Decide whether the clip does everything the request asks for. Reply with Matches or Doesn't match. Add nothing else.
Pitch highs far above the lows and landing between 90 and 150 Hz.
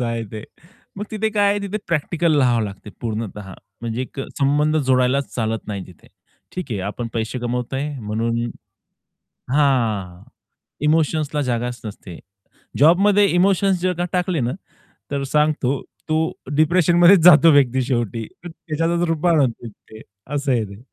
Matches